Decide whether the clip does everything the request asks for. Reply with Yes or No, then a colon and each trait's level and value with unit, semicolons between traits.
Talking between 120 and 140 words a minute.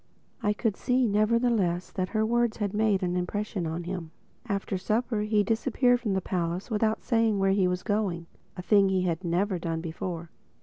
No: average, 180 wpm